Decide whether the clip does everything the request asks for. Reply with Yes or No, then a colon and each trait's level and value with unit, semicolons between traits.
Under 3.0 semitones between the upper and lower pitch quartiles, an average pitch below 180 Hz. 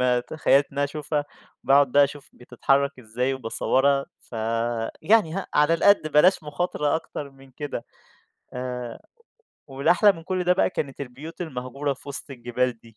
No: average, 3.4 semitones; medium, 140 Hz